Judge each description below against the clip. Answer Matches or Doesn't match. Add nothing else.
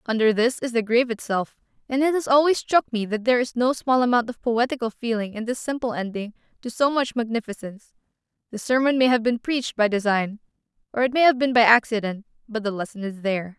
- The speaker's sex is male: Doesn't match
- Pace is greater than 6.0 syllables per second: Matches